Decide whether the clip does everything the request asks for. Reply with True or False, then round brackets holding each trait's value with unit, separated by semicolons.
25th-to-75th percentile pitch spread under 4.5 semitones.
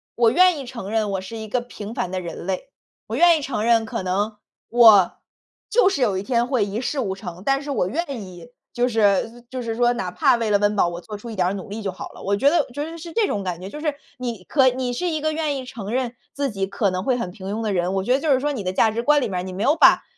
False (5.2 semitones)